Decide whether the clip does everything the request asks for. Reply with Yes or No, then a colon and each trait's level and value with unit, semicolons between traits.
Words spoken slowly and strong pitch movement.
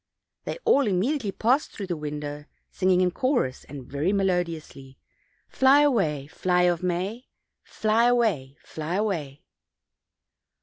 Yes: slow, 130 wpm; wide, 6.6 semitones